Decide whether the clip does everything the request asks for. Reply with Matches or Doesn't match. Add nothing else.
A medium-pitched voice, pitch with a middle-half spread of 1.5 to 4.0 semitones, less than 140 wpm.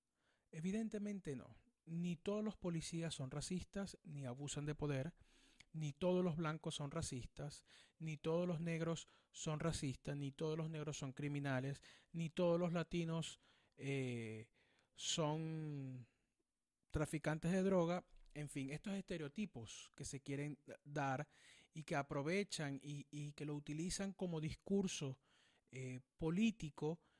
Matches